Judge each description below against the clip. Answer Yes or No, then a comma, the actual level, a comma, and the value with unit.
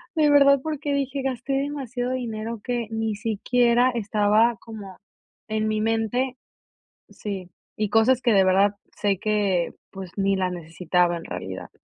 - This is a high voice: Yes, high, 220 Hz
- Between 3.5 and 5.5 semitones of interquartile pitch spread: Yes, average, 4.2 semitones